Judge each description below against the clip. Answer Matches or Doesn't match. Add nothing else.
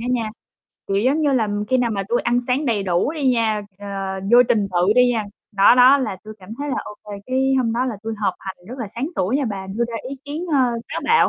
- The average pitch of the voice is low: Doesn't match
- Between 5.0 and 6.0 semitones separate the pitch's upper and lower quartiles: Doesn't match